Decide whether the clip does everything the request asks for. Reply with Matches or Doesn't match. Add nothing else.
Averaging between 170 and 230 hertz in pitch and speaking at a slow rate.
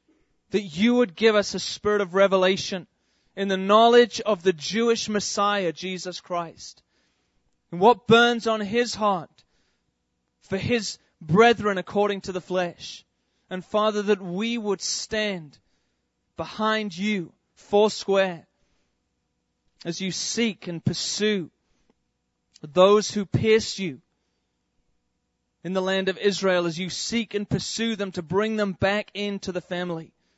Matches